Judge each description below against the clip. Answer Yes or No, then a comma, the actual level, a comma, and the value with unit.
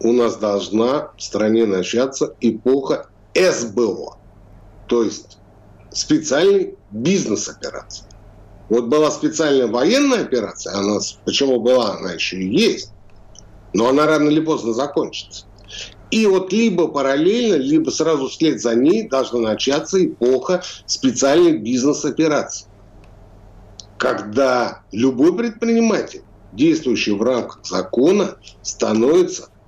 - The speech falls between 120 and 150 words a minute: No, slow, 110 wpm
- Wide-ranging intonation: Yes, wide, 7.3 semitones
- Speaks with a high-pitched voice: No, low, 120 Hz